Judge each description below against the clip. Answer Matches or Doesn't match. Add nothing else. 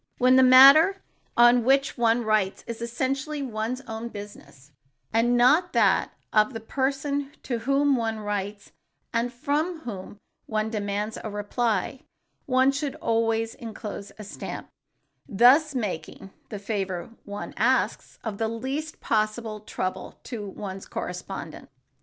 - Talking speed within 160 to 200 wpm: Doesn't match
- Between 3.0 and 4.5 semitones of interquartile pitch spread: Matches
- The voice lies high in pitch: Matches